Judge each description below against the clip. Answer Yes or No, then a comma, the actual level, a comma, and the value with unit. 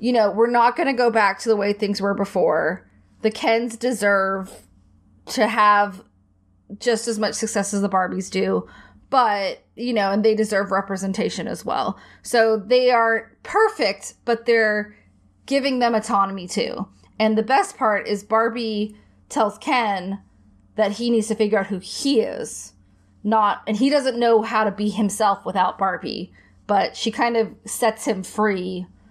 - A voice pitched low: No, high, 215 Hz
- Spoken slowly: No, average, 165 wpm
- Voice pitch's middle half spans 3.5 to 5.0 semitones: No, average, 2.8 semitones